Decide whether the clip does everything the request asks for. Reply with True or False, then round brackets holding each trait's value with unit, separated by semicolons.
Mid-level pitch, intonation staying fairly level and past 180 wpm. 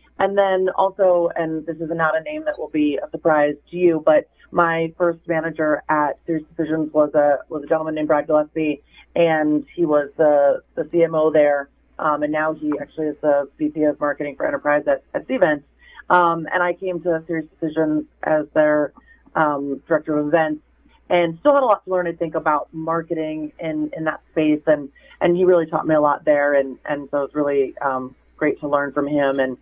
True (155 Hz; 2.2 semitones; 205 wpm)